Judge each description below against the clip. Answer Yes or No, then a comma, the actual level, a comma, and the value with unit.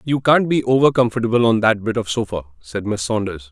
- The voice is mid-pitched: No, low, 120 Hz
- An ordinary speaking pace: No, fast, 220 wpm